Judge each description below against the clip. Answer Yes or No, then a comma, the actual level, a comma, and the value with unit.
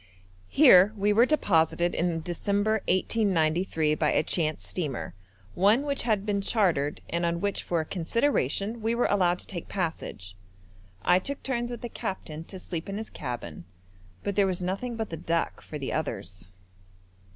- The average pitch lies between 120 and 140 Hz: No, medium, 185 Hz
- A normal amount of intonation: Yes, average, 4.9 semitones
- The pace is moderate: Yes, average, 170 wpm